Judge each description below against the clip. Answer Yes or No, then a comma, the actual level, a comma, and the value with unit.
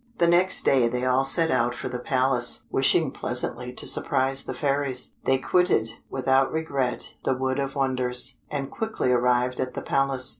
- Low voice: Yes, low, 130 Hz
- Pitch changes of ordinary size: No, narrow, 1.6 semitones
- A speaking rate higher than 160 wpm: Yes, average, 175 wpm